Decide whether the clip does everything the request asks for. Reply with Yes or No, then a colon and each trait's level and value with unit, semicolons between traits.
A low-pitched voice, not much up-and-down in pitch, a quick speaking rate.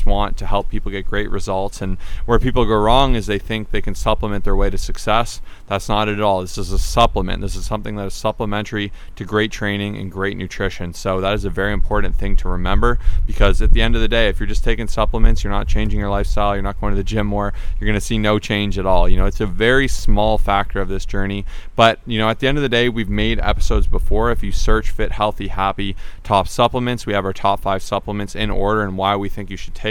Yes: low, 100 Hz; narrow, 1.9 semitones; fast, 260 wpm